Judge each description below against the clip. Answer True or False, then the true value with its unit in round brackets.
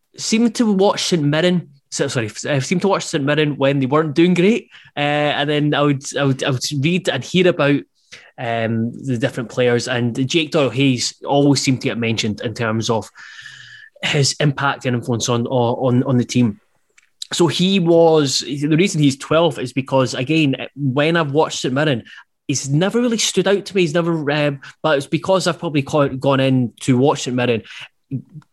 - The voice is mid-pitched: True (145 Hz)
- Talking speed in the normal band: True (195 wpm)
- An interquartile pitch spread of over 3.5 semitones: True (4.4 semitones)